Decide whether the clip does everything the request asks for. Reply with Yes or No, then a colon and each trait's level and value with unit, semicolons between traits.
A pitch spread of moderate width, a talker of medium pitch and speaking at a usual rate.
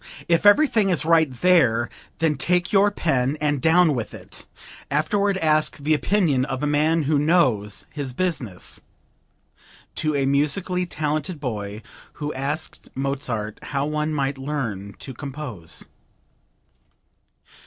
No: average, 3.8 semitones; medium, 150 Hz; slow, 130 wpm